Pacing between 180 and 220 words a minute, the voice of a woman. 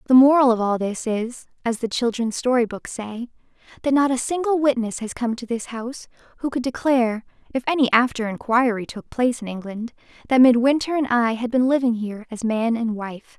Yes: average, 195 wpm; female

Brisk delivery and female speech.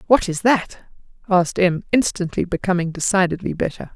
No: slow, 135 wpm; female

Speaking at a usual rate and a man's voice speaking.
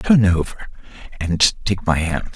Yes: average, 155 wpm; male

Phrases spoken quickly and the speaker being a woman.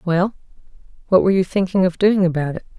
No: average, 170 wpm; female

